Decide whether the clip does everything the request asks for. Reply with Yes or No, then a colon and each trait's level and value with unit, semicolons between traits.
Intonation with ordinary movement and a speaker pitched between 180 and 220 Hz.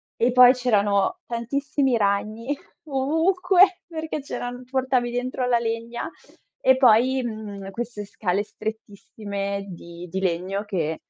No: average, 4.6 semitones; high, 235 Hz